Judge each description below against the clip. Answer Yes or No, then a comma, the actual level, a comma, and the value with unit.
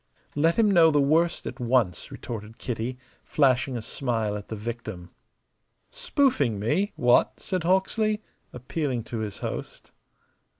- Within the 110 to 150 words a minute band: Yes, slow, 135 wpm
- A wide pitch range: Yes, wide, 7.0 semitones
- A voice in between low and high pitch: No, low, 125 Hz